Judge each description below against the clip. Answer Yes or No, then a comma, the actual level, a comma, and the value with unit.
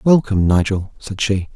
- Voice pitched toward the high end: No, low, 105 Hz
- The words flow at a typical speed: Yes, average, 155 wpm